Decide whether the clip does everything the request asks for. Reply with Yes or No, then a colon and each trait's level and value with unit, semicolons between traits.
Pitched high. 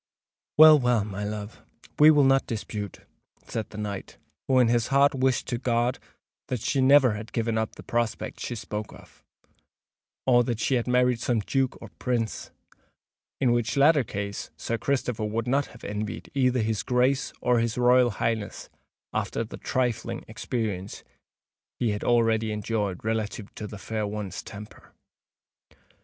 No: low, 115 Hz